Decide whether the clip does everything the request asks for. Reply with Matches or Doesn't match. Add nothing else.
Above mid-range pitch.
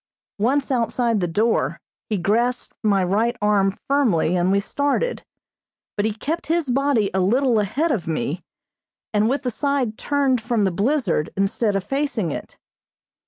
Matches